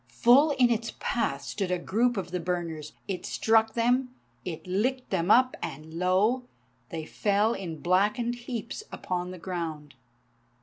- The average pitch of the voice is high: Yes, high, 195 Hz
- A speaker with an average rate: Yes, average, 155 wpm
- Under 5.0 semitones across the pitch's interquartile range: No, wide, 5.5 semitones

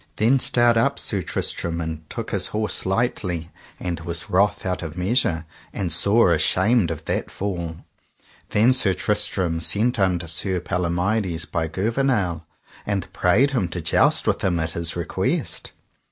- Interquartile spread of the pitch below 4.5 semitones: Yes, average, 4.0 semitones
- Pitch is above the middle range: No, very low, 90 Hz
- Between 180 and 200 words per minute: No, average, 155 wpm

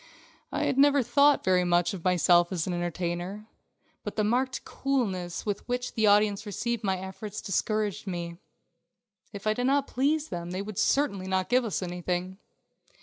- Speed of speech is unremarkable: Yes, average, 170 wpm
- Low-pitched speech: No, high, 200 Hz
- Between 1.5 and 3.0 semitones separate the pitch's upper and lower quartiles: No, average, 4.9 semitones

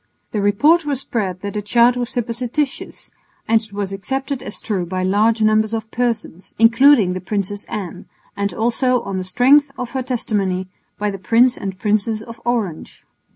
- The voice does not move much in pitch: No, average, 3.6 semitones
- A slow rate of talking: No, average, 175 wpm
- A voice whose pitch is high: Yes, high, 220 Hz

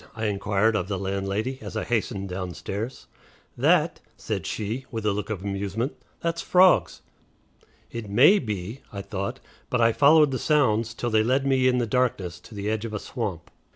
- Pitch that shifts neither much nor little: Yes, average, 4.2 semitones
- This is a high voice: No, low, 110 Hz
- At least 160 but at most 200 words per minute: Yes, average, 185 wpm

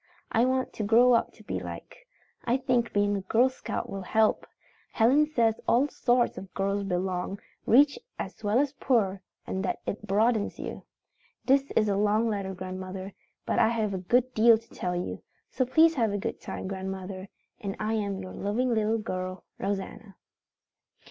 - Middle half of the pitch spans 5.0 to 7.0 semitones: No, average, 3.8 semitones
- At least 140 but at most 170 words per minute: No, average, 180 wpm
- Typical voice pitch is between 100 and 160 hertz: No, high, 215 Hz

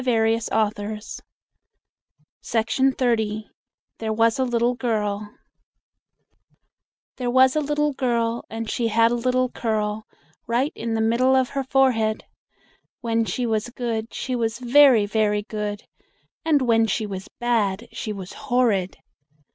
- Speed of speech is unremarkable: No, slow, 130 wpm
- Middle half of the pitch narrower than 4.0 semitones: Yes, narrow, 2.5 semitones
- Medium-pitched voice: No, high, 230 Hz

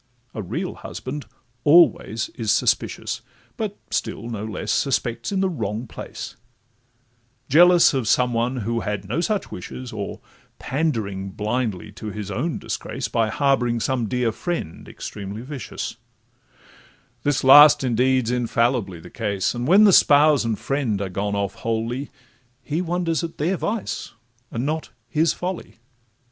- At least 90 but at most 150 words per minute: Yes, average, 145 wpm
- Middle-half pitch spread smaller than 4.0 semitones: No, wide, 5.4 semitones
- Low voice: Yes, low, 120 Hz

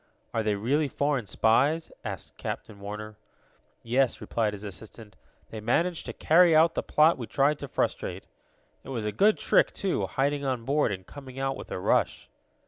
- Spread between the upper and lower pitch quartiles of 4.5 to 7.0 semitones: Yes, wide, 5.5 semitones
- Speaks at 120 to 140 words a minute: No, average, 180 wpm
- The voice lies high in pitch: No, low, 130 Hz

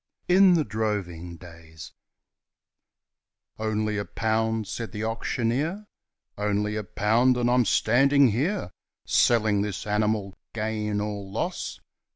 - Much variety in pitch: No, average, 2.7 semitones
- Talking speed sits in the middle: No, slow, 115 wpm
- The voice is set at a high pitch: No, low, 110 Hz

